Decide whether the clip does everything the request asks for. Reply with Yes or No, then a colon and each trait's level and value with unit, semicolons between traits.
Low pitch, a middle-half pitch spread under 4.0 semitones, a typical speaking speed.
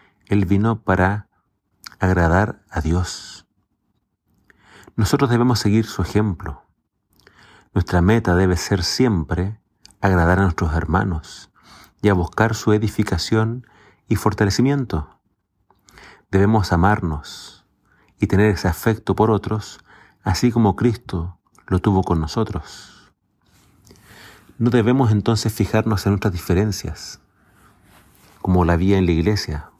No: low, 100 Hz; average, 3.3 semitones; slow, 110 wpm